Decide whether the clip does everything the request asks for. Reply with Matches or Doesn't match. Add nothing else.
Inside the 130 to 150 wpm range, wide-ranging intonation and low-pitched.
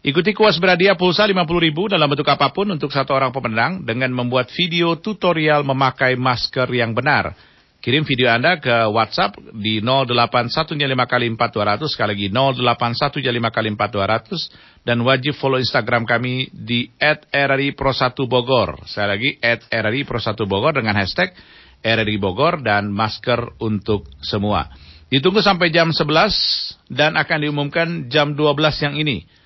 Doesn't match